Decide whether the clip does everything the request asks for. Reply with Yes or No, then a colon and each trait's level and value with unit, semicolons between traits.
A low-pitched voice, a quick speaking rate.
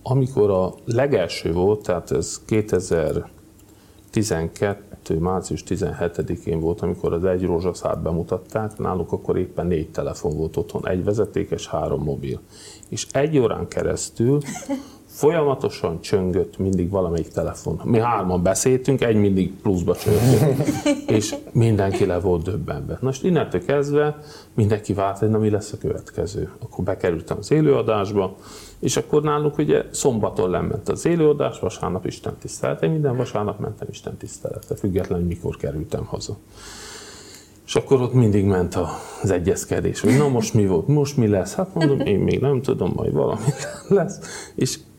No: low, 105 Hz; average, 145 wpm